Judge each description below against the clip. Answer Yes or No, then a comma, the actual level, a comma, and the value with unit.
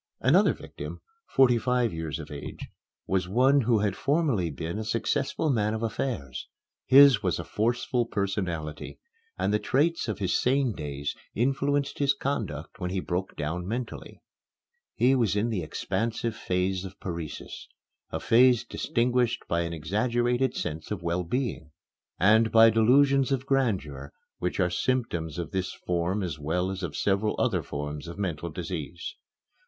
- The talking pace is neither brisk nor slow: Yes, average, 155 wpm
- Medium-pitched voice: No, low, 105 Hz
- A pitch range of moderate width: No, wide, 6.3 semitones